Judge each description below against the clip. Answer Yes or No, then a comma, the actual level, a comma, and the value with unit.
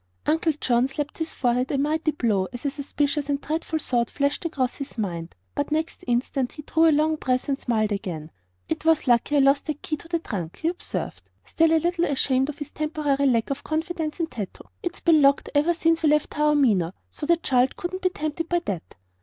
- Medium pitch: No, very high, 290 Hz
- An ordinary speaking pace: No, fast, 215 wpm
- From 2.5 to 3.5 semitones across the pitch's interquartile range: No, average, 4.1 semitones